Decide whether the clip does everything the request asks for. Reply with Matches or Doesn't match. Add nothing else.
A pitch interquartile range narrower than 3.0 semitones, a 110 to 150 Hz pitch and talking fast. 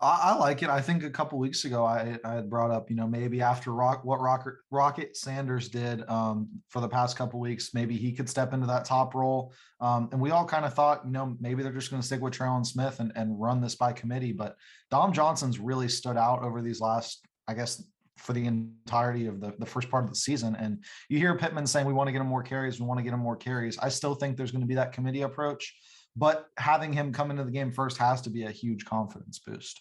Matches